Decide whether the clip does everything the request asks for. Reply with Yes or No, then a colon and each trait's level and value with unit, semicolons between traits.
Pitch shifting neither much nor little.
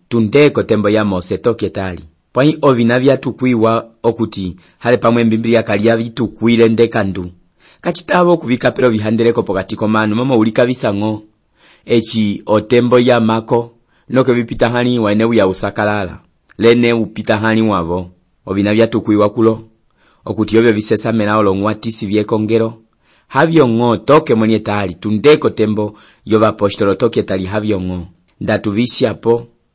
No: narrow, 2.0 semitones